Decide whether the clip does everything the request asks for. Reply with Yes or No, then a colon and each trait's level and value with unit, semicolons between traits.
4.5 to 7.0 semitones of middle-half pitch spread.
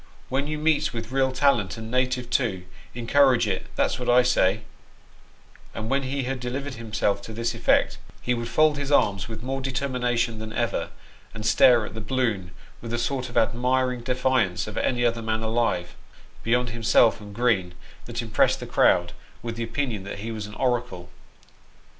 No: average, 2.7 semitones